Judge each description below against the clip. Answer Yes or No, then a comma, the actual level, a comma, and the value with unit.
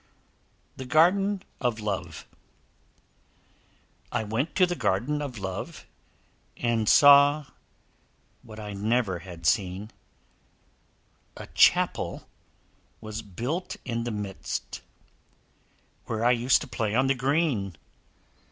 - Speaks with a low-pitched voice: Yes, low, 115 Hz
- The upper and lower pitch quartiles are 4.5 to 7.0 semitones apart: Yes, wide, 5.4 semitones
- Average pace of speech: No, slow, 105 wpm